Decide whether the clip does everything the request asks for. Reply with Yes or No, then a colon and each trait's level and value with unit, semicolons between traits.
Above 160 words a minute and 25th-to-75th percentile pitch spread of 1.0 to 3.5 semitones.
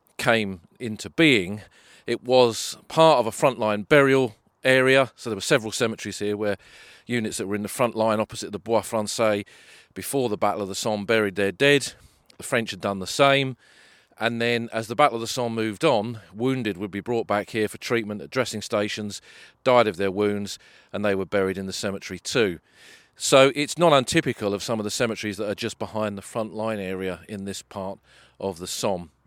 Yes: fast, 205 wpm; average, 3.0 semitones